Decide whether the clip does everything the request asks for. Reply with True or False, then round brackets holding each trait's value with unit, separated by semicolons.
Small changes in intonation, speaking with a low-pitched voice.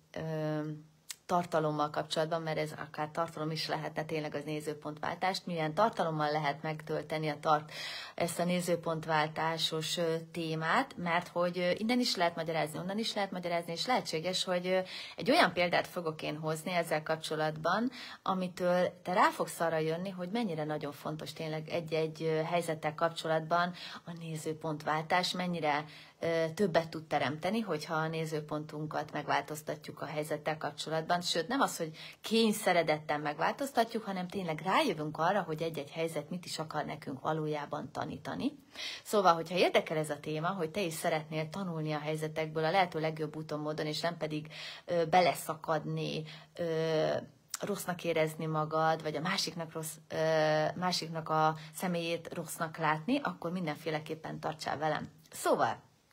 False (2.3 semitones; 160 Hz)